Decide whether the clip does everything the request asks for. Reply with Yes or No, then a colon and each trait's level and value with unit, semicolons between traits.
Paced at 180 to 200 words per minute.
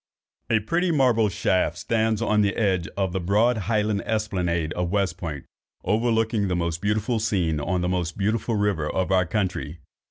No: average, 170 wpm